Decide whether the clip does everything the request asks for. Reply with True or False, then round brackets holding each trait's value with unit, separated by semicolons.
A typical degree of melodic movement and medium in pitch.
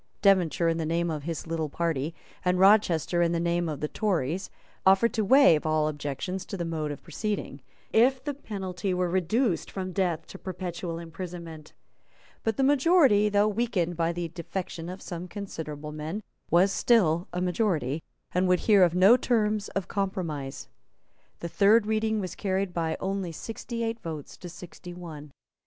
True (3.6 semitones; 180 Hz)